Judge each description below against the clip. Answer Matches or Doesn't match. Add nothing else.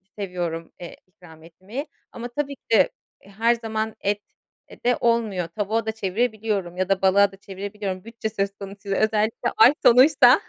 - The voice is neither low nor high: Doesn't match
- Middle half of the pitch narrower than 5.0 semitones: Matches